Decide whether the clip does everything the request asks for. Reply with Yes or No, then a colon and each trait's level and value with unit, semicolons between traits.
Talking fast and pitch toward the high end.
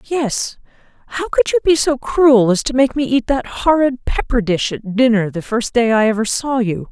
Yes: fast, 215 wpm; high, 245 Hz